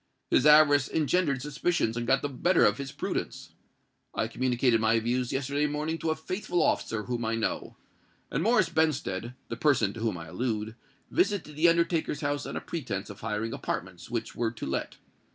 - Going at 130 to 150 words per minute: No, average, 175 wpm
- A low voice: Yes, low, 130 Hz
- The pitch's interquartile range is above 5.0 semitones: Yes, wide, 5.4 semitones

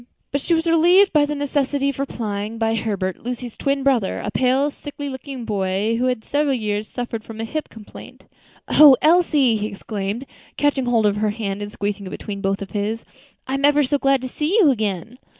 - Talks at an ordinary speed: No, fast, 210 wpm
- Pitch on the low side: No, high, 245 Hz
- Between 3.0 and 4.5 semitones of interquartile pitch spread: No, average, 5.3 semitones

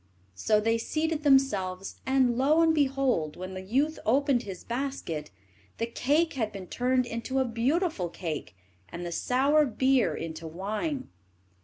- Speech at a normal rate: Yes, average, 150 wpm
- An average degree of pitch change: No, wide, 6.5 semitones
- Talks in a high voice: Yes, high, 245 Hz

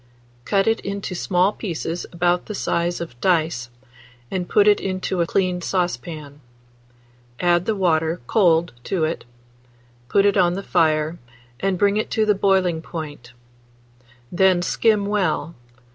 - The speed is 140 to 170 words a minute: Yes, average, 145 wpm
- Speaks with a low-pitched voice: No, medium, 180 Hz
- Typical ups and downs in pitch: Yes, average, 3.0 semitones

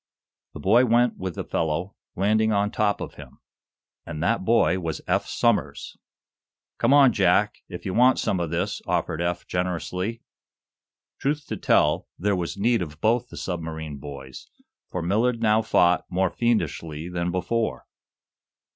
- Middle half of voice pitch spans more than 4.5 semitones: Yes, average, 5.0 semitones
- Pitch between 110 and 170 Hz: No, very low, 95 Hz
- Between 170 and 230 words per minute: No, average, 155 wpm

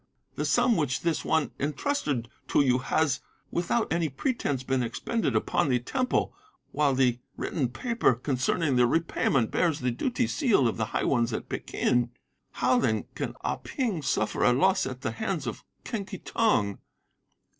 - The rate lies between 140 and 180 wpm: Yes, average, 165 wpm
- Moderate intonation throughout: No, wide, 6.5 semitones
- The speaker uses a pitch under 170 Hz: Yes, medium, 140 Hz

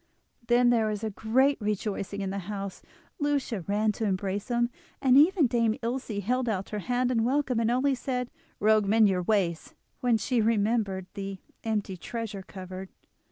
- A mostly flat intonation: No, average, 3.7 semitones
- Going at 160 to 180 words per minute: Yes, average, 165 wpm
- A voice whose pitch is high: Yes, high, 220 Hz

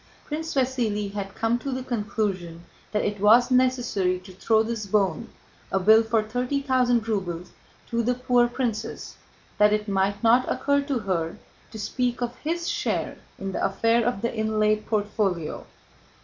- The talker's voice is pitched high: Yes, high, 220 Hz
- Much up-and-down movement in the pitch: No, average, 3.5 semitones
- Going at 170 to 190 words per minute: No, average, 155 wpm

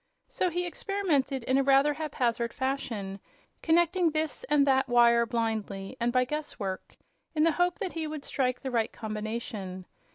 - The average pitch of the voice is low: No, very high, 265 Hz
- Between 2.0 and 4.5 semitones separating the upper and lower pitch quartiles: No, average, 5.0 semitones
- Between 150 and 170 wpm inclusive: Yes, average, 160 wpm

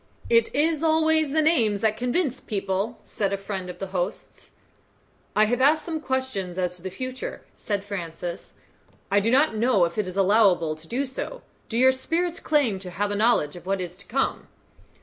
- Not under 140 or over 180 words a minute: No, average, 195 wpm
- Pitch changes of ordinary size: No, wide, 5.7 semitones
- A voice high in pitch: Yes, high, 215 Hz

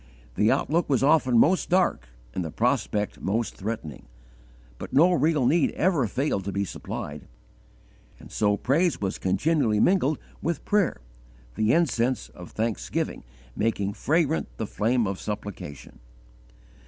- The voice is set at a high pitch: No, low, 115 Hz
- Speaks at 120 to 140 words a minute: Yes, slow, 135 wpm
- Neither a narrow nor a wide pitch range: No, wide, 7.7 semitones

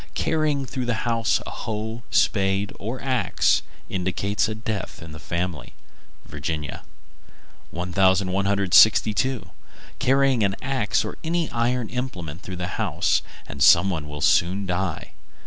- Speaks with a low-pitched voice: Yes, low, 100 Hz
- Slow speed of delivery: Yes, slow, 130 wpm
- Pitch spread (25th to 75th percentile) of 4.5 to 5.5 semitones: Yes, average, 5.1 semitones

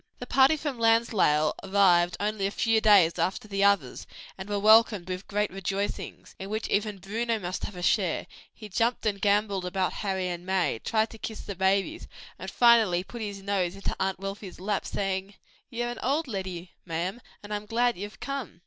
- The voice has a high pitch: Yes, high, 200 Hz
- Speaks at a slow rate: No, average, 195 wpm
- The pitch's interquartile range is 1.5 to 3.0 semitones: Yes, average, 2.7 semitones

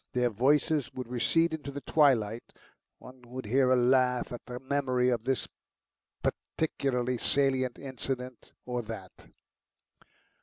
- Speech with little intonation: Yes, narrow, 1.9 semitones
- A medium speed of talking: No, slow, 125 wpm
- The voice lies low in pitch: Yes, low, 125 Hz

